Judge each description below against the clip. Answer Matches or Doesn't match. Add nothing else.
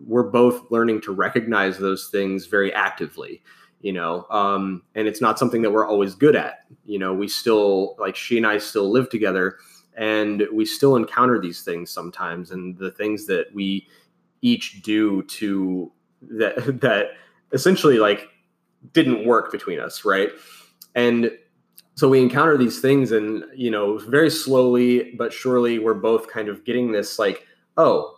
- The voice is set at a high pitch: Doesn't match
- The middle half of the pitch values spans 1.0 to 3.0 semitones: Doesn't match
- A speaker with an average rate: Matches